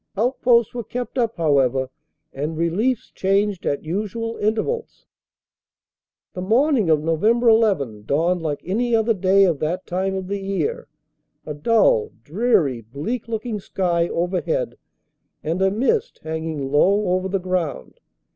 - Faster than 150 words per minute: No, average, 145 wpm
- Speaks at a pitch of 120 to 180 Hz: No, high, 190 Hz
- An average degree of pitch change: No, wide, 6.0 semitones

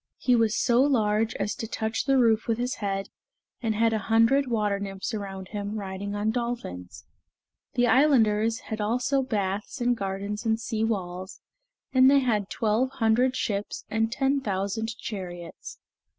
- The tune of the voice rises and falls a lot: No, average, 3.2 semitones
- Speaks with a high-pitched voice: Yes, high, 220 Hz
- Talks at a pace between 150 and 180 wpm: Yes, average, 160 wpm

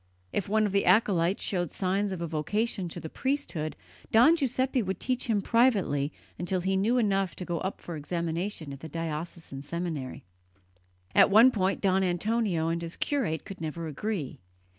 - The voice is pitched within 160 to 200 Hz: Yes, medium, 185 Hz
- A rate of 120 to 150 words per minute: No, average, 175 wpm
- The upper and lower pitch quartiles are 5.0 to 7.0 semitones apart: No, average, 4.3 semitones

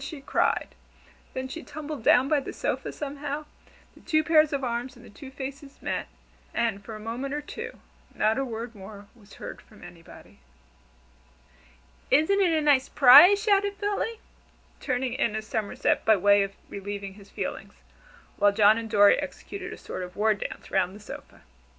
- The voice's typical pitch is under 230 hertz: No, very high, 255 Hz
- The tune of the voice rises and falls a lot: Yes, wide, 5.8 semitones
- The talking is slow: No, average, 170 wpm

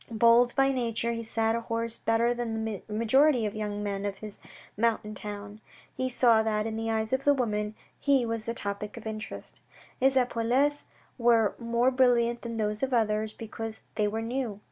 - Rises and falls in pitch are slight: Yes, narrow, 2.0 semitones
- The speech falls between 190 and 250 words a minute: Yes, average, 195 wpm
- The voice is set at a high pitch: Yes, high, 225 Hz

